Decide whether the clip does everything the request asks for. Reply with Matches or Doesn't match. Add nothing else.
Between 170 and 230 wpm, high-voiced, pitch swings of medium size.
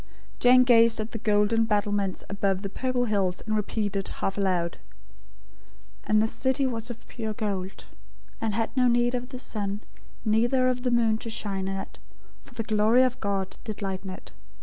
Matches